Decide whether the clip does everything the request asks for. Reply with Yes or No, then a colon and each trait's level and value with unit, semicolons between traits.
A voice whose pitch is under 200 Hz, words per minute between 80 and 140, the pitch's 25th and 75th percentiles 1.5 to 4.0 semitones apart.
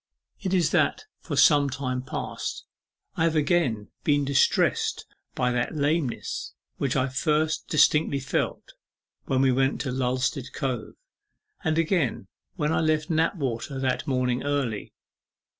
Yes: medium, 140 Hz; slow, 135 wpm; average, 3.4 semitones